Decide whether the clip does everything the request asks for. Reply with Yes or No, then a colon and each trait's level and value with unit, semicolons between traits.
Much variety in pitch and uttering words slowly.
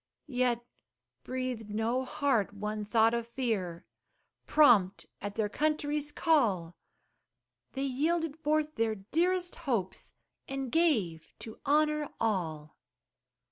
Yes: wide, 6.2 semitones; slow, 105 wpm